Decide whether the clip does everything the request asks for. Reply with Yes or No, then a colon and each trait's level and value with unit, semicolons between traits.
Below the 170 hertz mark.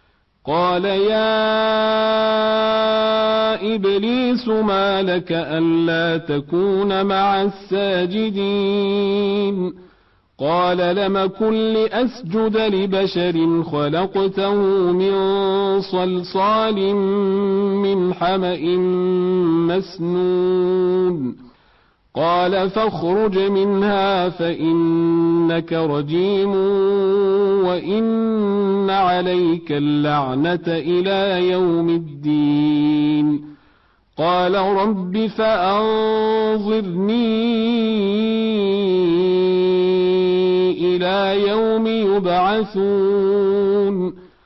No: high, 195 Hz